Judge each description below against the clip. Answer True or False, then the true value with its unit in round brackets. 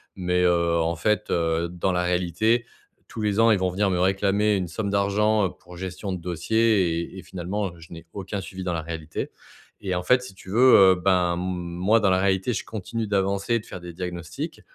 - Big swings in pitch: False (2.7 semitones)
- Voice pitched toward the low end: True (95 Hz)